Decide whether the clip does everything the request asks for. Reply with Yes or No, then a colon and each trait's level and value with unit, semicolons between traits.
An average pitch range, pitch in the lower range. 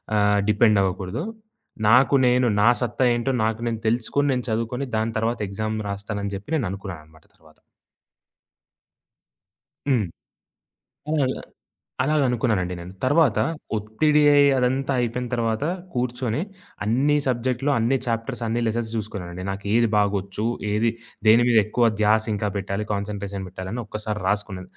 Yes: average, 3.4 semitones; low, 110 Hz